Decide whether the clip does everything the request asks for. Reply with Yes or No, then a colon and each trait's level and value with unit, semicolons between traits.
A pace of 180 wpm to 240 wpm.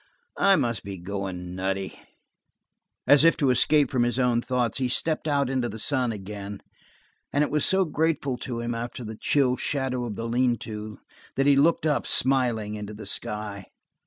Yes: average, 185 wpm